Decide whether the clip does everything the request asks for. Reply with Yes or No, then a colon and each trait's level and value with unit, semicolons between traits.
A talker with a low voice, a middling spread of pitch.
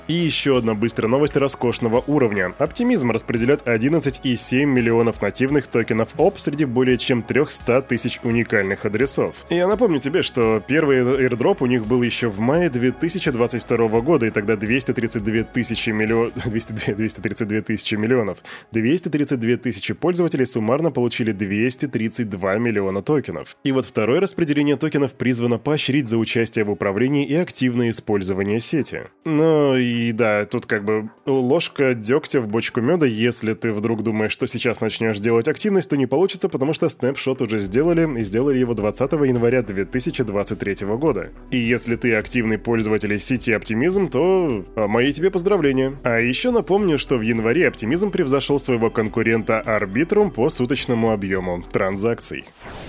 Yes: low, 120 Hz; average, 3.7 semitones